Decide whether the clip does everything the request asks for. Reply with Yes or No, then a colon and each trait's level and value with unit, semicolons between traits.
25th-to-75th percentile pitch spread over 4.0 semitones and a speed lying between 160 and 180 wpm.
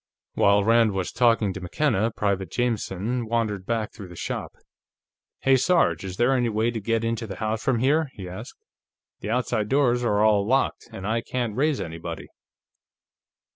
No: average, 3.3 semitones; average, 165 wpm